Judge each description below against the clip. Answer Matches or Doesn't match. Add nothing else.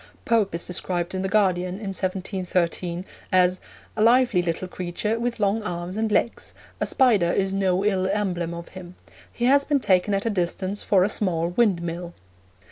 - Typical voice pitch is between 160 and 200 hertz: Matches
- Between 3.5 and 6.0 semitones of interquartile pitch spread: Doesn't match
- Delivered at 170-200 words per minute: Matches